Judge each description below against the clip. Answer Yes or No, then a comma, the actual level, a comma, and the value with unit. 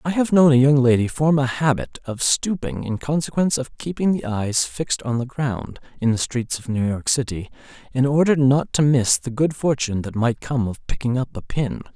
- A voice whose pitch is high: No, low, 130 Hz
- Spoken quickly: Yes, fast, 220 wpm